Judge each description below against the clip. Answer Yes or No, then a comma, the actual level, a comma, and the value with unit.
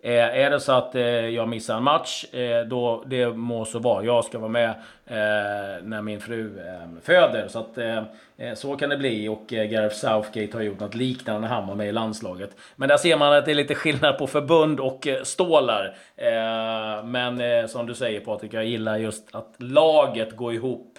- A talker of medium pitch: No, low, 115 Hz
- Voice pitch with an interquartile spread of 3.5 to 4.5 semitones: No, average, 2.8 semitones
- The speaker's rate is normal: No, fast, 210 wpm